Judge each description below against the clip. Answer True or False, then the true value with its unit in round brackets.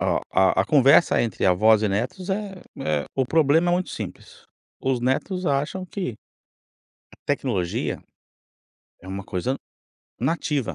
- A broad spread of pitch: True (7.8 semitones)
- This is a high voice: False (135 Hz)